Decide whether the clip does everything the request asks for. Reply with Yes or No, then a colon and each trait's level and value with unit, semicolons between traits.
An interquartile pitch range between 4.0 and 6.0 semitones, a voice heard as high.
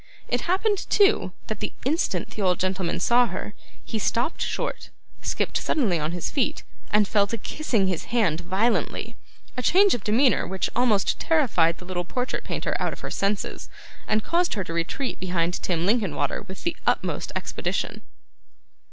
Yes: wide, 5.6 semitones; high, 210 Hz